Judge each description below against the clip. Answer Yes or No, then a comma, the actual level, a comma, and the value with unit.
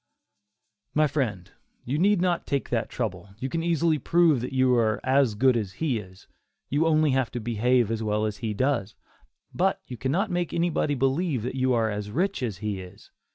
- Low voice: Yes, low, 130 Hz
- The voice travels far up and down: Yes, wide, 6.0 semitones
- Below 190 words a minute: No, average, 200 wpm